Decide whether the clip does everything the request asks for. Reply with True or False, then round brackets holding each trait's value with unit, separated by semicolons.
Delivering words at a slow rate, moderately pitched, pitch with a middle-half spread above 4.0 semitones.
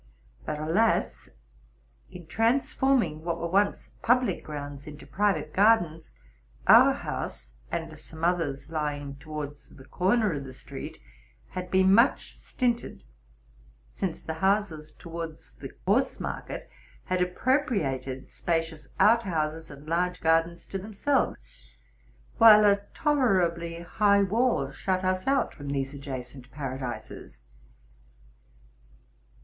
True (115 wpm; 170 Hz; 5.3 semitones)